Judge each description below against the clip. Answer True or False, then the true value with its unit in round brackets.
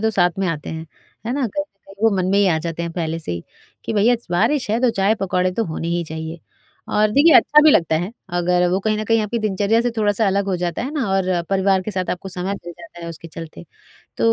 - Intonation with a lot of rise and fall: False (4.1 semitones)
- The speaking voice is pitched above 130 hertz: True (190 Hz)